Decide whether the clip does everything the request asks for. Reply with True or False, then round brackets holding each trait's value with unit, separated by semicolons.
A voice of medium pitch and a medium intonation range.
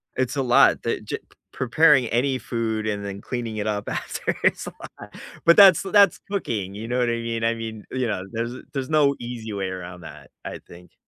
False (115 Hz; 3.6 semitones)